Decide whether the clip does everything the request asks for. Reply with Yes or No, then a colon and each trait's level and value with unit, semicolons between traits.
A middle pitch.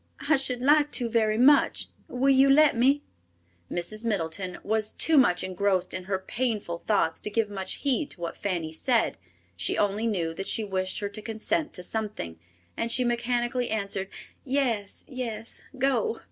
No: high, 220 Hz